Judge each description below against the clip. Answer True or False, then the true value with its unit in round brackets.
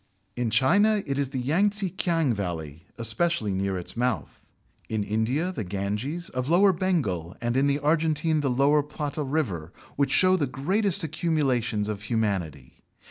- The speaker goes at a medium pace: True (160 wpm)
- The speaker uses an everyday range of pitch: False (7.4 semitones)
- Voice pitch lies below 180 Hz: True (135 Hz)